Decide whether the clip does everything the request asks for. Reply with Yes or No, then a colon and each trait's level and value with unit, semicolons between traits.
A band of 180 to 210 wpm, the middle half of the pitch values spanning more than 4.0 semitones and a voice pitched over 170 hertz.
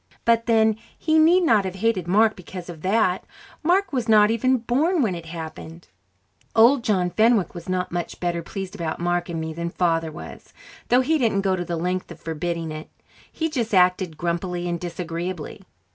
Yes: average, 190 wpm; average, 5.0 semitones; medium, 185 Hz